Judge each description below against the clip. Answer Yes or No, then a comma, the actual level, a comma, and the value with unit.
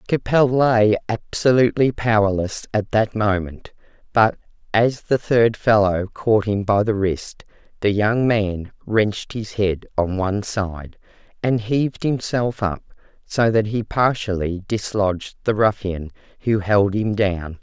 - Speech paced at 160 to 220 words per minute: No, average, 140 wpm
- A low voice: Yes, low, 105 Hz